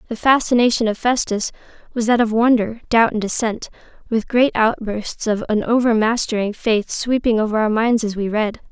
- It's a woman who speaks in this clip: Yes, female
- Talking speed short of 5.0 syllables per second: No, 5.1 syllables/s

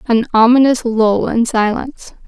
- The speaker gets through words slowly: Yes, slow, 130 wpm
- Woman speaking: Yes, female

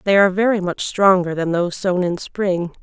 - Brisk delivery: Yes, fast, 215 wpm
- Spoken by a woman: Yes, female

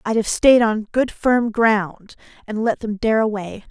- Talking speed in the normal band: Yes, average, 195 wpm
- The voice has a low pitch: No, high, 220 Hz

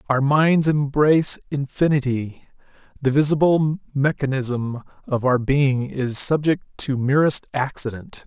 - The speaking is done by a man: Yes, male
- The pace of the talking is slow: Yes, slow, 110 wpm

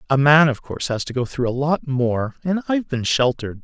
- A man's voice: Yes, male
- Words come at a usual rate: No, fast, 250 wpm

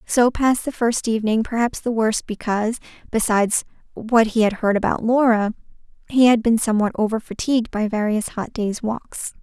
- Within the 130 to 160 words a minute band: No, average, 170 wpm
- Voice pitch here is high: Yes, high, 225 Hz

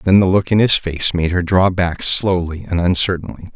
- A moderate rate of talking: No, fast, 220 wpm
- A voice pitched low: Yes, very low, 90 Hz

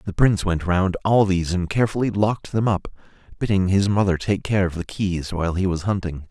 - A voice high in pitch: No, very low, 95 Hz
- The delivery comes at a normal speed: No, fast, 220 wpm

